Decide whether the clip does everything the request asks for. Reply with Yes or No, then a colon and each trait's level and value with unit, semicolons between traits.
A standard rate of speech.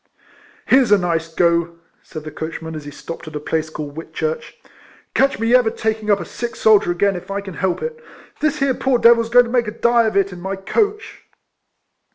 No: fast, 230 wpm